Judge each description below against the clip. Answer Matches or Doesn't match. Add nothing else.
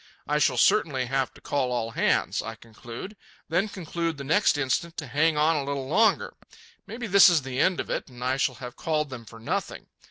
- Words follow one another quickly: Matches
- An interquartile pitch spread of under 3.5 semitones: Doesn't match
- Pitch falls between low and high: Matches